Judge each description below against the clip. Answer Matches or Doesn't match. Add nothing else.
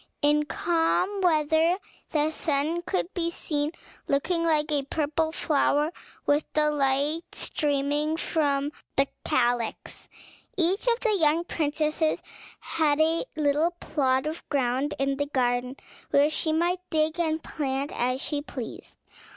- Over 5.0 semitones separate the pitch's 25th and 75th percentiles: Doesn't match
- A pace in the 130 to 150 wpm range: Matches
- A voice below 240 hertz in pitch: Doesn't match